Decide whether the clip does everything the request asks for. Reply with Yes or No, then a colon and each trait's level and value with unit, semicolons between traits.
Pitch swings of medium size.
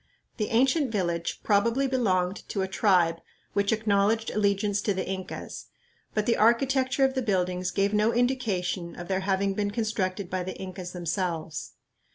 Yes: average, 3.5 semitones